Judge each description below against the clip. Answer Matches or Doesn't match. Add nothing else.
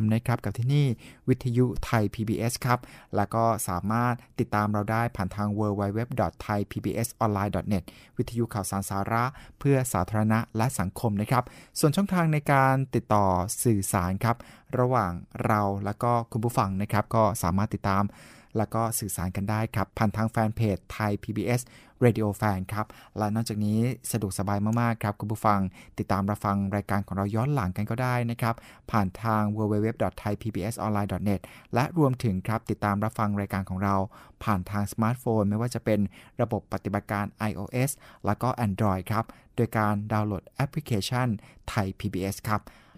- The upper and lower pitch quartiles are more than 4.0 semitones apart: Doesn't match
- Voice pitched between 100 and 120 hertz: Matches